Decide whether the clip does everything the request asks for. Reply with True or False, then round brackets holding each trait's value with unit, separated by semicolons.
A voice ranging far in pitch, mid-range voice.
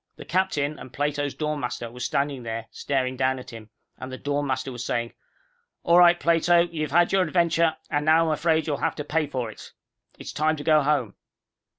False (3.8 semitones; 145 Hz)